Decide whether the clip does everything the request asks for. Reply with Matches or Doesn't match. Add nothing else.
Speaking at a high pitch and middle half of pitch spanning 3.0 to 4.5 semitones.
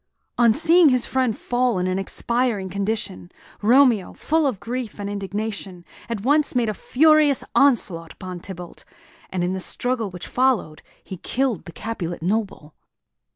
Doesn't match